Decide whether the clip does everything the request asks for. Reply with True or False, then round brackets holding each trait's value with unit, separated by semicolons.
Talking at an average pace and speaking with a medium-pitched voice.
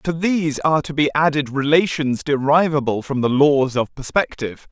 True (165 wpm; 145 Hz)